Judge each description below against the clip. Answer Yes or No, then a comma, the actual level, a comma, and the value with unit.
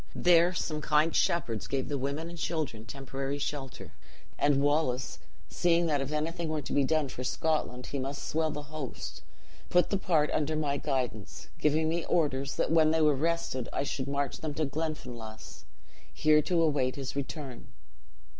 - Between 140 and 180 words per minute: Yes, average, 175 wpm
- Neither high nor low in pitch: Yes, medium, 150 Hz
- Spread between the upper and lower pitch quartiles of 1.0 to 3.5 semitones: Yes, average, 2.8 semitones